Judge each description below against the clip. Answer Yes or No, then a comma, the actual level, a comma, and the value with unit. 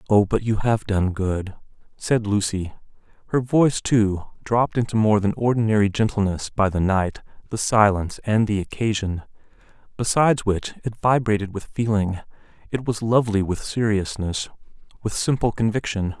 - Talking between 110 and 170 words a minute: Yes, average, 145 wpm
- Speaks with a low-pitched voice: Yes, low, 105 Hz